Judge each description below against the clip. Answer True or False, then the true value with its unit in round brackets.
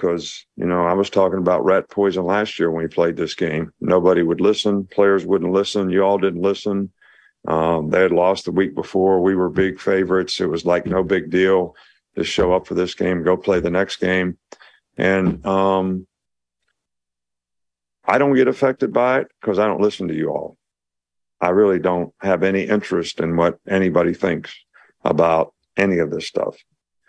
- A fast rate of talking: False (185 wpm)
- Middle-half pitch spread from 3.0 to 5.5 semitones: False (2.4 semitones)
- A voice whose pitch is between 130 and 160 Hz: False (95 Hz)